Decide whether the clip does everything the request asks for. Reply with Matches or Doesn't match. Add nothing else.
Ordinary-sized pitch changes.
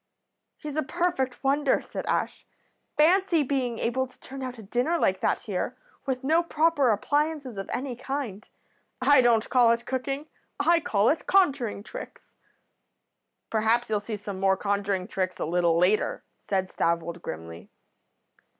Doesn't match